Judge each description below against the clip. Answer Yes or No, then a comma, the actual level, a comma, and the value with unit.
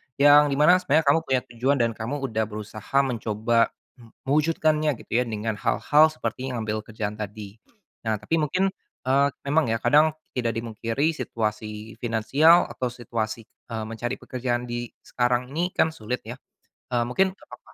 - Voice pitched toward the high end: No, low, 120 Hz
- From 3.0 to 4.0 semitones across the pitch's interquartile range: No, average, 4.8 semitones